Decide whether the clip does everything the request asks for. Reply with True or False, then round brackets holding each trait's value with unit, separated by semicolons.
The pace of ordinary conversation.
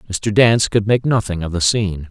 False (230 wpm)